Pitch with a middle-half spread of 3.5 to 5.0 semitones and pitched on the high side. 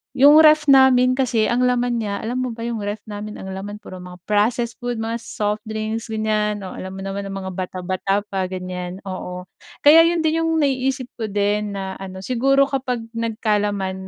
Yes: average, 4.3 semitones; high, 215 Hz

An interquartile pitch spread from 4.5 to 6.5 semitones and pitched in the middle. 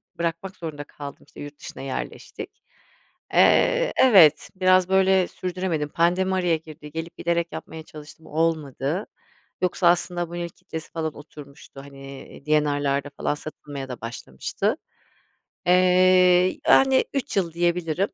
No: average, 3.7 semitones; medium, 165 Hz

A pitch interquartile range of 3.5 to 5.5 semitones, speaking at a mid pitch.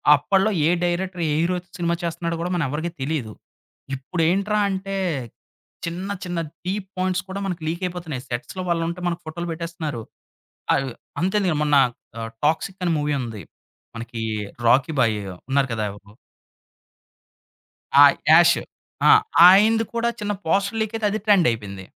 Yes: average, 5.1 semitones; medium, 170 Hz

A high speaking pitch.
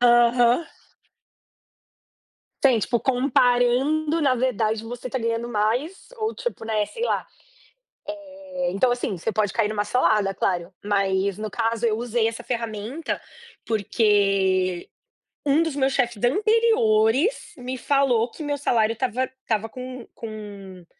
Yes: high, 235 Hz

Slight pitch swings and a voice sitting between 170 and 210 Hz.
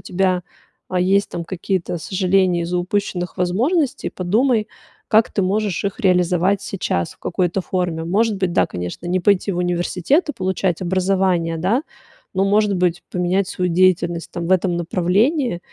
Yes: narrow, 2.1 semitones; medium, 185 Hz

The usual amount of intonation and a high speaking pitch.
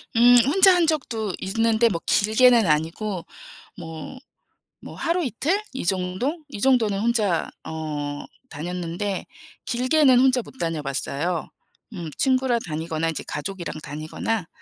No: wide, 7.5 semitones; high, 205 Hz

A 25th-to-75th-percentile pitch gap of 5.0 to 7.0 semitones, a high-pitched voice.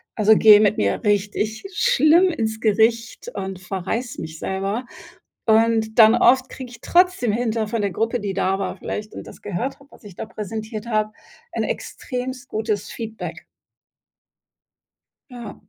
No: average, 2.7 semitones; high, 220 Hz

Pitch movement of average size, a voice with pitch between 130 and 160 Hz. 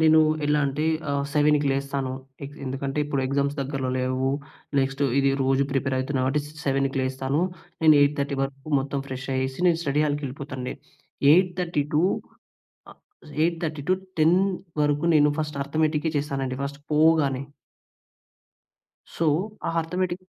No: narrow, 2.2 semitones; medium, 140 Hz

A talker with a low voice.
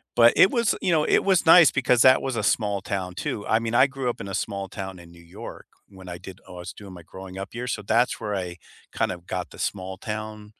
Yes: low, 105 Hz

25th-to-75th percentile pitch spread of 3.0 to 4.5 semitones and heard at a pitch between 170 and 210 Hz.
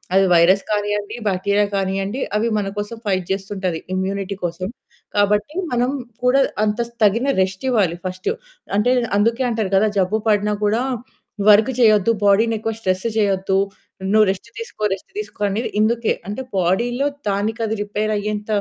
No: narrow, 2.6 semitones; high, 205 Hz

